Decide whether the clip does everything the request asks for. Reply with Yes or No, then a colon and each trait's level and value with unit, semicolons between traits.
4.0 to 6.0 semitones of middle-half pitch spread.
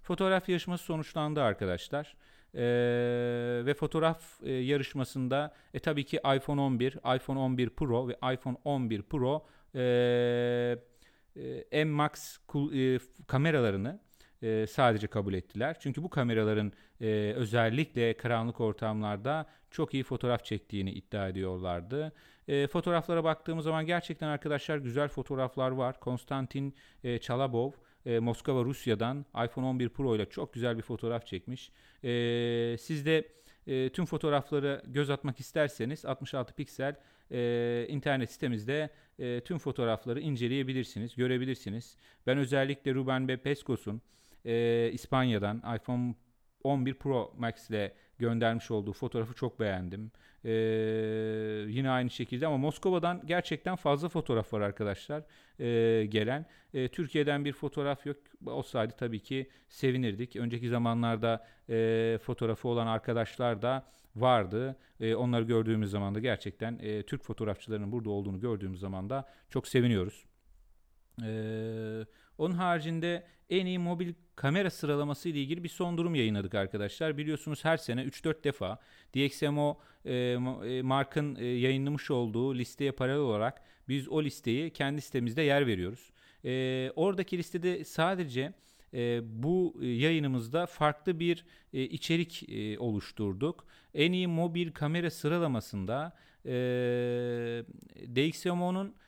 Yes: average, 4.3 semitones